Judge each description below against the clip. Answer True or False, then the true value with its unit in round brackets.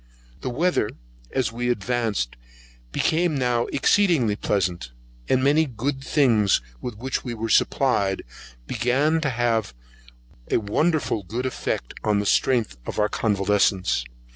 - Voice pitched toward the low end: True (120 Hz)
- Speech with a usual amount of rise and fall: True (4.5 semitones)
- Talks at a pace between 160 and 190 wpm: False (135 wpm)